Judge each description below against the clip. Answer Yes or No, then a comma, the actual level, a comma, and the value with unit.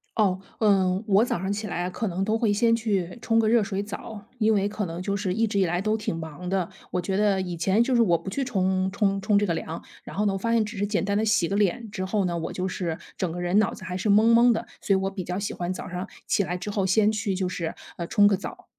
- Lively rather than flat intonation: No, average, 2.7 semitones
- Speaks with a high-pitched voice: Yes, high, 195 Hz